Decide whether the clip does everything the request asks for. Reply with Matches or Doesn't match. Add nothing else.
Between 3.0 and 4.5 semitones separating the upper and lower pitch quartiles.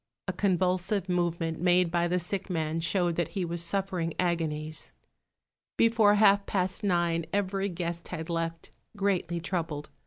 Doesn't match